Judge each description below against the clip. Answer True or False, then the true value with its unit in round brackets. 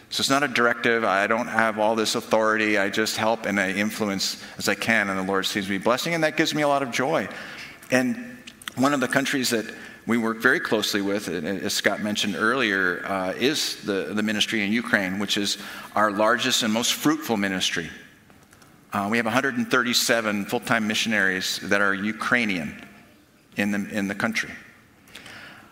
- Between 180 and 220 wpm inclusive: True (185 wpm)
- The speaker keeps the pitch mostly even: False (3.4 semitones)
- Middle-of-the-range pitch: False (110 Hz)